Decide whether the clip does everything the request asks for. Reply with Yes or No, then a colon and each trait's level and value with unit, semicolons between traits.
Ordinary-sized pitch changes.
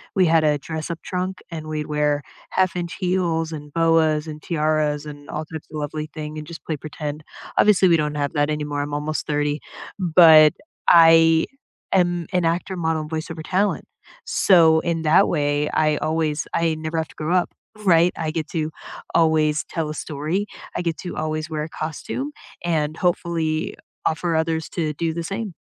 No: narrow, 1.8 semitones